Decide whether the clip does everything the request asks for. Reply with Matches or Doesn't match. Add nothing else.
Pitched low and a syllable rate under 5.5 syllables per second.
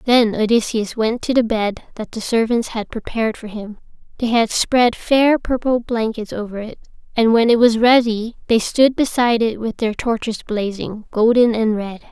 Doesn't match